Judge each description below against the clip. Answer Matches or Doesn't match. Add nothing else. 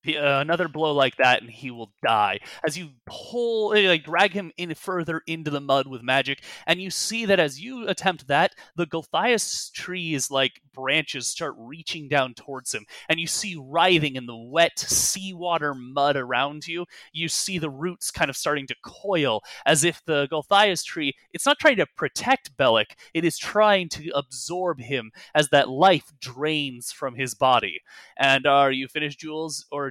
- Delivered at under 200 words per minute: Matches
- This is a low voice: Doesn't match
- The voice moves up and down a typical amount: Matches